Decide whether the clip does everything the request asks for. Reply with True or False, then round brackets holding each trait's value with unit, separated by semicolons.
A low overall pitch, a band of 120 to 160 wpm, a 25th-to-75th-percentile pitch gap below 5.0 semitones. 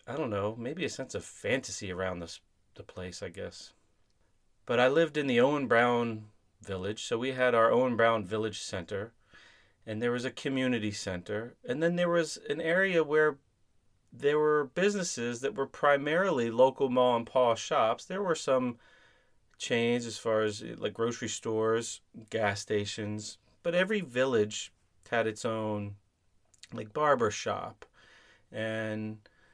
True (115 Hz; 155 wpm; 4.0 semitones)